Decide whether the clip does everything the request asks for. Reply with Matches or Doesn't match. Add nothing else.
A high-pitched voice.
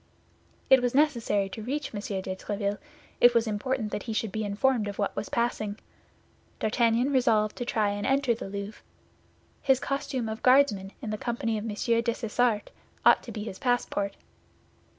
Matches